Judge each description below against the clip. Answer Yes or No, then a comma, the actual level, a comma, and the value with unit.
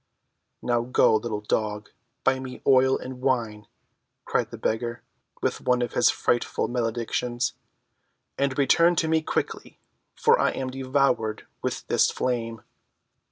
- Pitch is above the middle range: No, low, 125 Hz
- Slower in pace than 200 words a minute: Yes, slow, 135 wpm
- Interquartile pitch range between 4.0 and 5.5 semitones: No, narrow, 2.5 semitones